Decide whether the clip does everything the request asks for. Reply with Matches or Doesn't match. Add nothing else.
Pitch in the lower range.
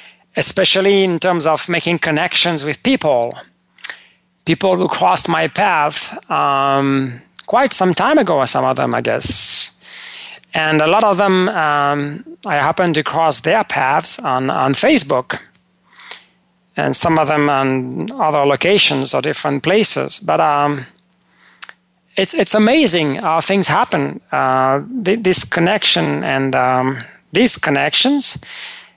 Doesn't match